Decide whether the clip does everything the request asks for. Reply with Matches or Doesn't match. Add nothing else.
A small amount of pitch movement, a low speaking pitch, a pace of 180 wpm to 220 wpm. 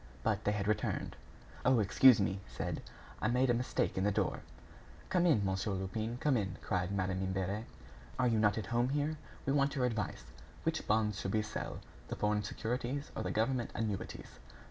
Doesn't match